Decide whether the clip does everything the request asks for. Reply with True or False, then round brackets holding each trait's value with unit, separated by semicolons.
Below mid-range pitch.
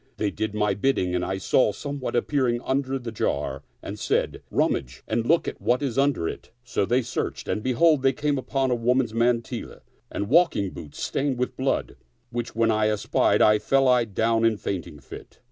True (120 Hz)